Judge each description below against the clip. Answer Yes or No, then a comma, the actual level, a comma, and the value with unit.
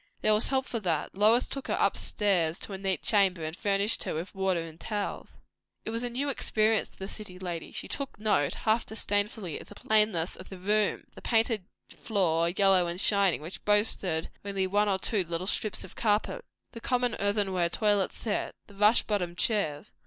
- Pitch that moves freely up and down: No, average, 3.1 semitones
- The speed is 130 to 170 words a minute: No, average, 190 wpm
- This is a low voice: No, high, 200 Hz